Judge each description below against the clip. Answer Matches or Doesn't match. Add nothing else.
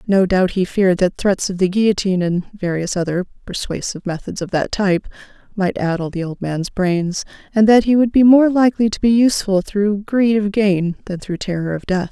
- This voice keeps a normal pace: Doesn't match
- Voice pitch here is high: Matches